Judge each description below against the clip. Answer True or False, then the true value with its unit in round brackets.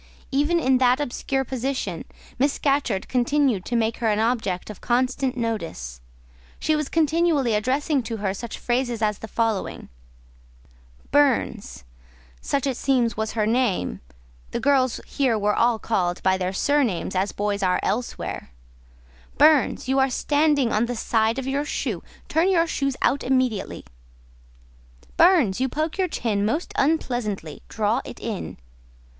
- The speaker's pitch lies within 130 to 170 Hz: False (245 Hz)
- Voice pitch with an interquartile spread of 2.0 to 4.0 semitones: False (4.6 semitones)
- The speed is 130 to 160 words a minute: True (150 wpm)